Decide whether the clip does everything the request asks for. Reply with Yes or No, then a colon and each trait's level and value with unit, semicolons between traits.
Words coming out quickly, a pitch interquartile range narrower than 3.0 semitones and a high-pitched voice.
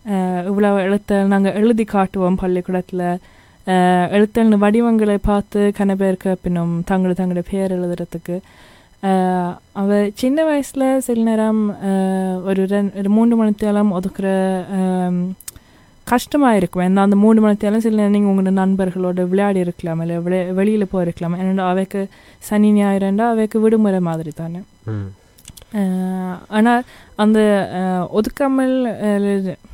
No: average, 105 wpm; narrow, 2.4 semitones; high, 195 Hz